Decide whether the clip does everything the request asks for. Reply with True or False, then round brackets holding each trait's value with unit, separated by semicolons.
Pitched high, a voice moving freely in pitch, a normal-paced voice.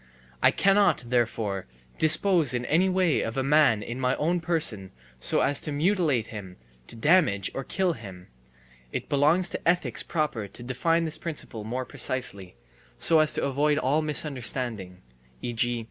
False (135 Hz; 5.9 semitones; 160 wpm)